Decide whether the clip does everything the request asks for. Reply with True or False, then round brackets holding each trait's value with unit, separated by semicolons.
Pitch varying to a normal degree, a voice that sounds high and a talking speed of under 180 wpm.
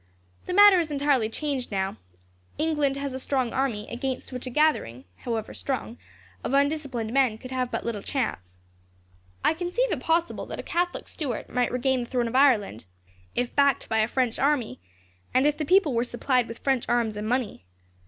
False (3.6 semitones; 255 Hz; 185 wpm)